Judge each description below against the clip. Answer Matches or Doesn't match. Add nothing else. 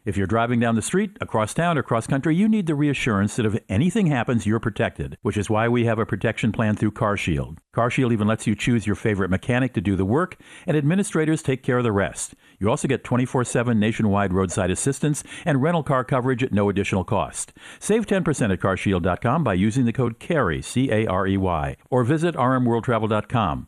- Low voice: Matches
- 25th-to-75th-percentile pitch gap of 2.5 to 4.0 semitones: Doesn't match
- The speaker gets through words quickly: Matches